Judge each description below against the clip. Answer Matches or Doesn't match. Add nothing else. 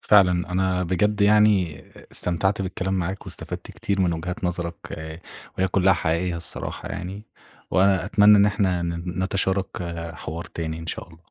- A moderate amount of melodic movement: Doesn't match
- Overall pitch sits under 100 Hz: Matches